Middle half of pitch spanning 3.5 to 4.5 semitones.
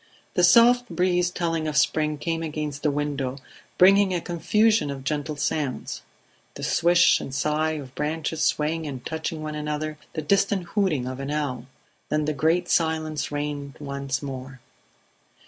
No: average, 2.9 semitones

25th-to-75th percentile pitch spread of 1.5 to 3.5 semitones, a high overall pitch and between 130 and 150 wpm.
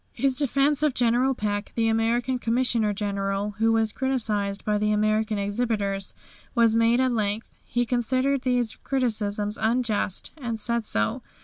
Yes: average, 2.9 semitones; high, 225 Hz; average, 145 wpm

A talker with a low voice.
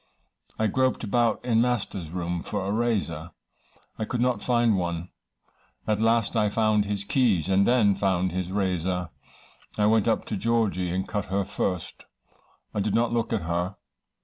Yes: low, 100 Hz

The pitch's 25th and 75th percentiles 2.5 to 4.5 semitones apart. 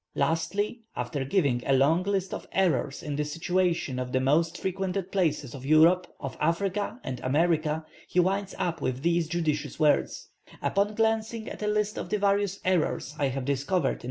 No: average, 5.2 semitones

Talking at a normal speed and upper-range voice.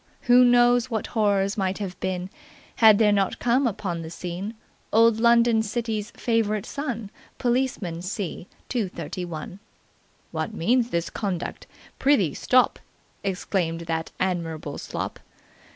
No: slow, 120 wpm; high, 205 Hz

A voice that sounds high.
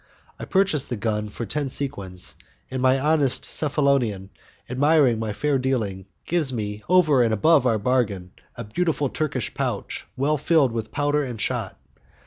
No: low, 130 Hz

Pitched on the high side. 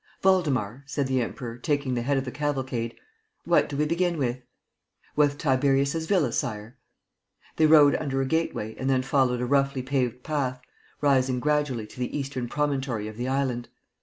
No: low, 135 Hz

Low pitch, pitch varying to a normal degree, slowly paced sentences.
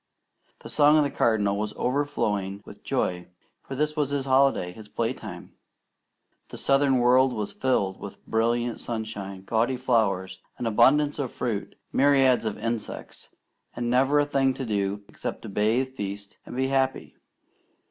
No: low, 120 Hz; average, 4.5 semitones; average, 155 wpm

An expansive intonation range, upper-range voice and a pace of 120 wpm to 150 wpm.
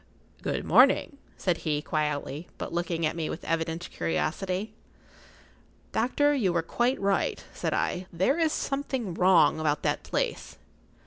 No: wide, 5.8 semitones; medium, 175 Hz; average, 140 wpm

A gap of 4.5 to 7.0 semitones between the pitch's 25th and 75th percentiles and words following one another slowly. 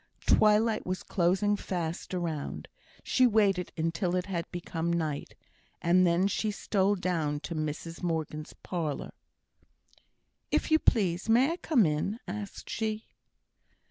No: average, 3.9 semitones; slow, 130 wpm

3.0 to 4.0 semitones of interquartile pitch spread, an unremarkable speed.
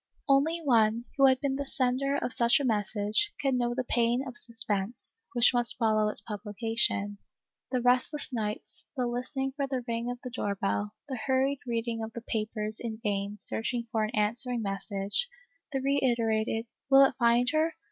Yes: average, 3.4 semitones; average, 180 wpm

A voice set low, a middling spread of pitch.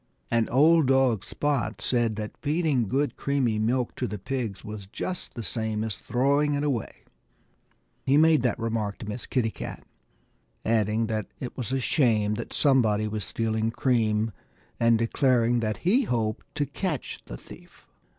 Yes: low, 115 Hz; average, 3.8 semitones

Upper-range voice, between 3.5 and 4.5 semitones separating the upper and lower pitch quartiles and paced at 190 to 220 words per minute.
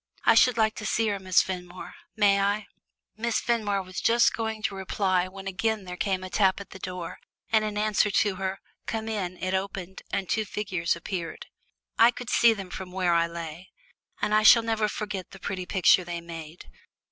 No: high, 195 Hz; average, 2.8 semitones; average, 200 wpm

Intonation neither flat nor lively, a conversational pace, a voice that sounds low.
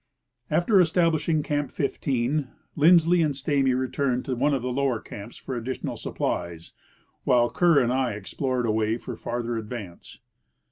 Yes: average, 4.0 semitones; average, 150 wpm; low, 130 Hz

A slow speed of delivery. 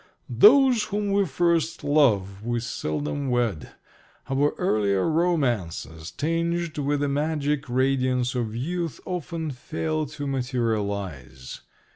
Yes: slow, 110 wpm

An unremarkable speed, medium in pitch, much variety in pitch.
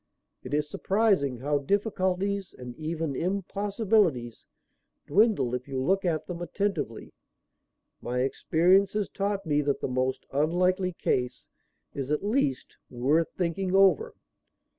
No: slow, 125 wpm; medium, 170 Hz; wide, 6.2 semitones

